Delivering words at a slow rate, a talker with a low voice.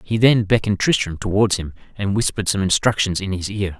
No: fast, 205 wpm; low, 100 Hz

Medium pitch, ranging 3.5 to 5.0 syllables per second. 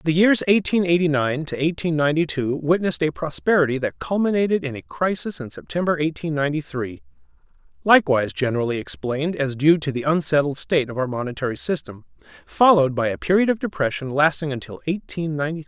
Yes: medium, 145 Hz; 4.6 syllables/s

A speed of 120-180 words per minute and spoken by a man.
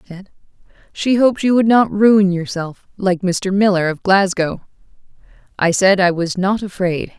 No: average, 165 wpm; female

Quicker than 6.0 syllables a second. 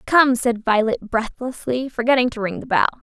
No: 5.2 syllables/s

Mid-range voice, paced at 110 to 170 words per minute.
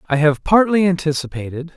Yes: medium, 160 Hz; slow, 135 wpm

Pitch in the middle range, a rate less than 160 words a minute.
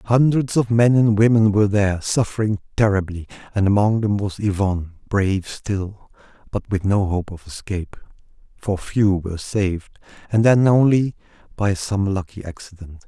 No: low, 100 Hz; average, 150 wpm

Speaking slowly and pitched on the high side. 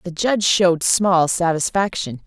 No: slow, 130 wpm; medium, 180 Hz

